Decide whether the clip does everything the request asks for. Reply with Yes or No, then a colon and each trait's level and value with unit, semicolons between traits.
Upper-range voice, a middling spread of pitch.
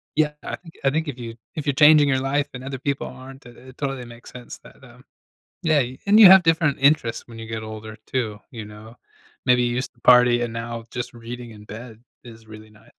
No: low, 125 Hz; average, 3.5 semitones